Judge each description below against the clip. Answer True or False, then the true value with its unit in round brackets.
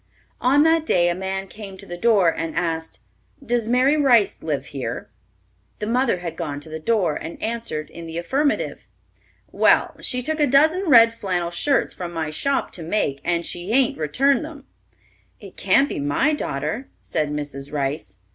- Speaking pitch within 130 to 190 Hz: True (185 Hz)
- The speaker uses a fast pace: False (175 wpm)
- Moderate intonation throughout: False (8.1 semitones)